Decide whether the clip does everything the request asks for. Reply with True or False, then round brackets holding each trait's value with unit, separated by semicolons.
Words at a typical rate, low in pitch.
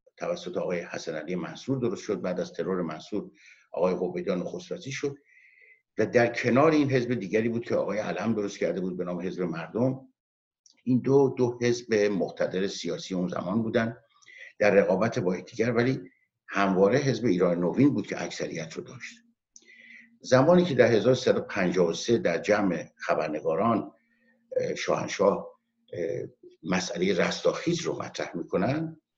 True (140 wpm; 130 Hz)